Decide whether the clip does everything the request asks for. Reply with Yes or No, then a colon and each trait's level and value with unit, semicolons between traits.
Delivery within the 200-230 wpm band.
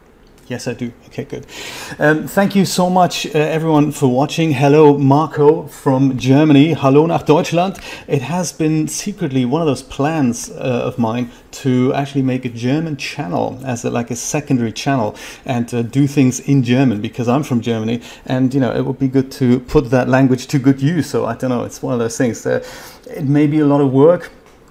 Yes: fast, 205 wpm